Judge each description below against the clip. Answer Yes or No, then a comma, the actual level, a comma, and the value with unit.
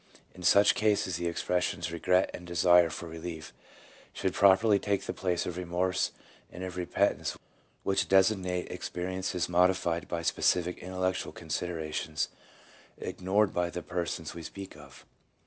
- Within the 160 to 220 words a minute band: No, average, 140 wpm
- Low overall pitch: Yes, very low, 90 Hz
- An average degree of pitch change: No, narrow, 1.5 semitones